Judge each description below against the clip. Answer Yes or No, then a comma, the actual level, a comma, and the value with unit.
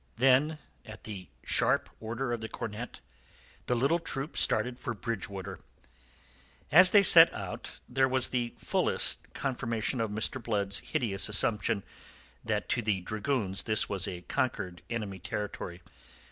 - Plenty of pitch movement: No, average, 4.1 semitones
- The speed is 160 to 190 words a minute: No, average, 140 wpm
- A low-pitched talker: Yes, low, 110 Hz